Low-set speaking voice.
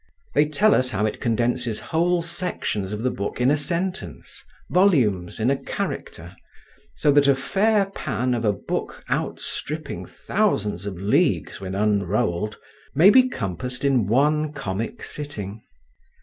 Yes: low, 130 Hz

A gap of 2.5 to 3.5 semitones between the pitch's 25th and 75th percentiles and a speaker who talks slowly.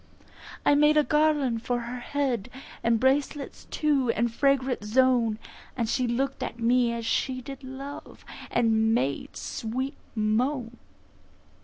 Yes: average, 3.0 semitones; slow, 130 wpm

